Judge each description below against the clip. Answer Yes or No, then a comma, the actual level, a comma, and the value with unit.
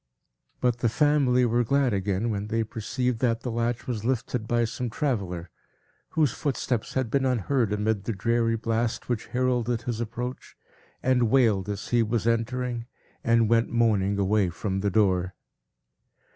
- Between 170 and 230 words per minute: No, average, 160 wpm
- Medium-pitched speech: No, low, 115 Hz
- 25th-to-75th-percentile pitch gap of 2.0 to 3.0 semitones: Yes, narrow, 2.5 semitones